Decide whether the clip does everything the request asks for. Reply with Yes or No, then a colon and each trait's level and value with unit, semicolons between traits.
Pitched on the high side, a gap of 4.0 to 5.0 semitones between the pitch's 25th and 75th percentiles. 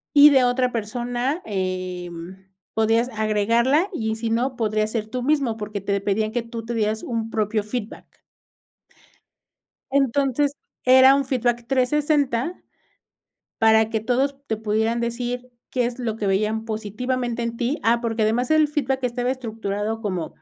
No: high, 230 Hz; average, 2.8 semitones